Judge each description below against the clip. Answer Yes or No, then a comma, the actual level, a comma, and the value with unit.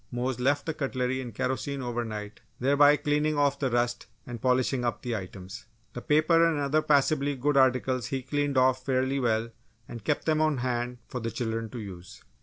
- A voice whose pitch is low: Yes, low, 130 Hz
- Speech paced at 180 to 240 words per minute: Yes, average, 195 wpm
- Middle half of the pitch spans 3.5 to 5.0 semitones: No, average, 3.0 semitones